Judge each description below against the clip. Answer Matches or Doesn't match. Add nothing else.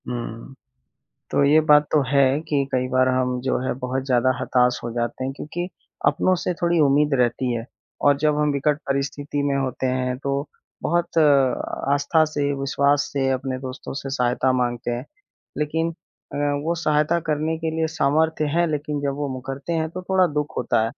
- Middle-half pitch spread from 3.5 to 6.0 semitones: Doesn't match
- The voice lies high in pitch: Doesn't match